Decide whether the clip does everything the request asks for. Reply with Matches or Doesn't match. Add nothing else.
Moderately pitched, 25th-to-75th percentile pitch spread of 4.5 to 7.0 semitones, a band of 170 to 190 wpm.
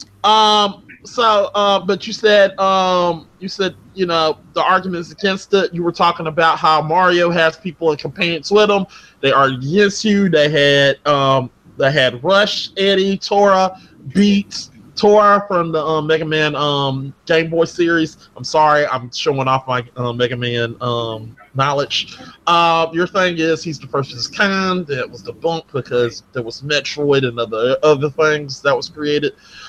Matches